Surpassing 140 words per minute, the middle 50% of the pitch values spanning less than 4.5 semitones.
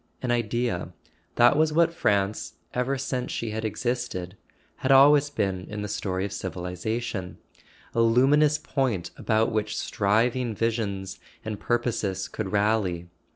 No: slow, 135 wpm; average, 4.0 semitones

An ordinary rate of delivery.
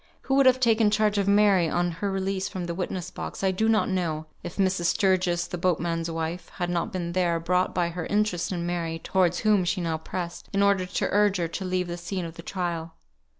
No: fast, 230 wpm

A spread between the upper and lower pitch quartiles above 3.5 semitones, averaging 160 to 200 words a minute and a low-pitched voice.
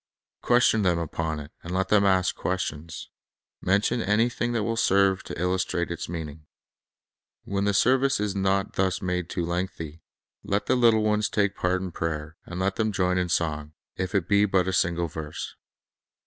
No: average, 3.1 semitones; average, 175 wpm; very low, 95 Hz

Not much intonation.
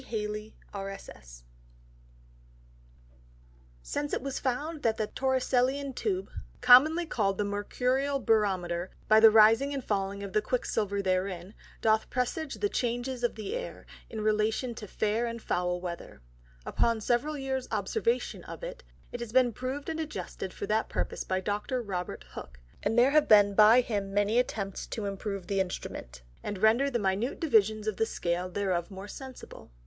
No: average, 4.5 semitones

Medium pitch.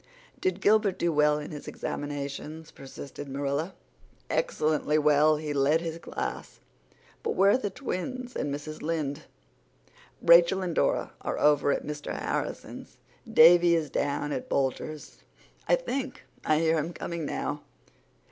Yes: medium, 155 Hz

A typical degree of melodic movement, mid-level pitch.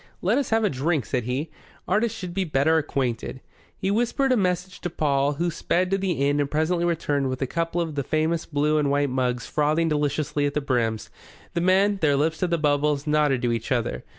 Yes: average, 3.9 semitones; medium, 150 Hz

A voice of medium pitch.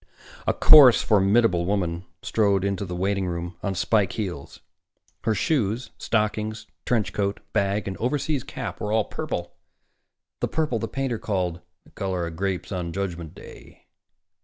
No: low, 100 Hz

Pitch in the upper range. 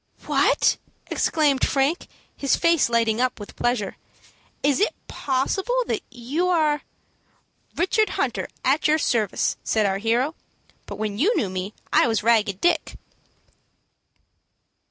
Yes: very high, 255 Hz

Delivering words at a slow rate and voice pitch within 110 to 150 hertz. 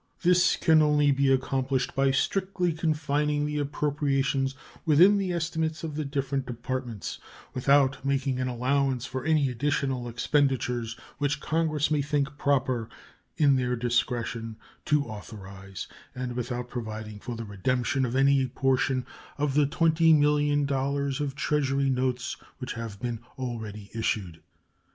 Yes: slow, 130 wpm; low, 135 Hz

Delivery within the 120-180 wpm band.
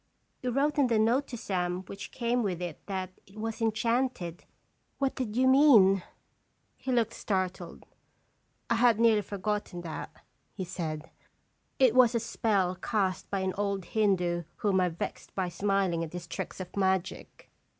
Yes: average, 175 wpm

